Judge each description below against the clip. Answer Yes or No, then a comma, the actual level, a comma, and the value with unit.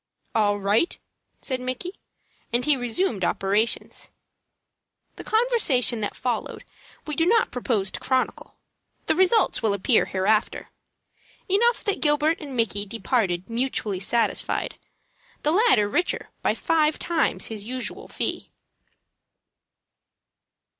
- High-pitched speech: Yes, very high, 250 Hz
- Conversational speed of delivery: No, slow, 120 wpm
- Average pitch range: No, wide, 7.3 semitones